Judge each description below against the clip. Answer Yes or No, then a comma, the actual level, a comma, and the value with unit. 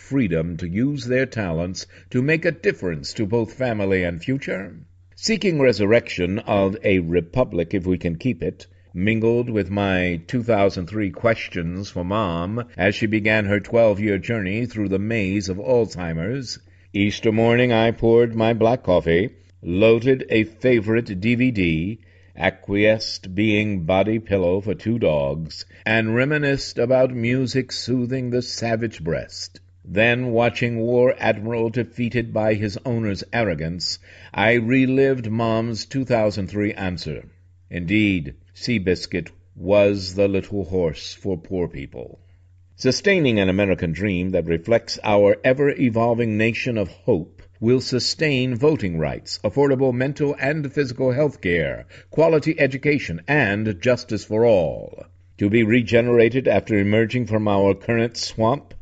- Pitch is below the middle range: Yes, low, 110 Hz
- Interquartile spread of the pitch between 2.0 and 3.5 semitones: No, average, 4.5 semitones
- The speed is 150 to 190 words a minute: No, slow, 135 wpm